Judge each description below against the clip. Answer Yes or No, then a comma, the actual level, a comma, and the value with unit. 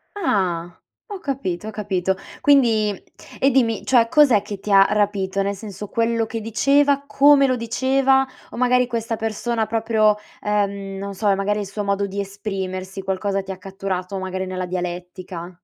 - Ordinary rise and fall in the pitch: Yes, average, 3.2 semitones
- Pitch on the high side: Yes, high, 205 Hz